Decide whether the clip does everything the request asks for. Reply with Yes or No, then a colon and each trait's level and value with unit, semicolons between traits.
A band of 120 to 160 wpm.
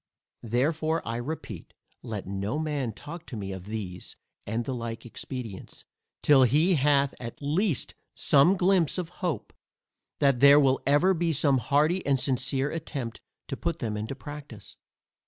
Yes: average, 155 wpm